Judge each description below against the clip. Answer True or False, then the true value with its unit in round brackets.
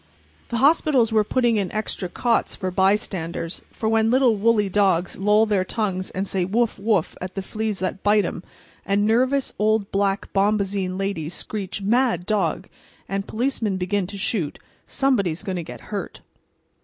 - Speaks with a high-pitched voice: True (200 Hz)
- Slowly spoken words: False (170 wpm)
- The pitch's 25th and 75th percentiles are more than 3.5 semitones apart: False (2.8 semitones)